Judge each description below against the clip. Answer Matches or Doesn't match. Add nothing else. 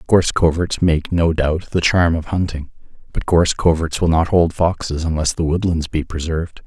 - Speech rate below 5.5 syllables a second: Matches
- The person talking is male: Matches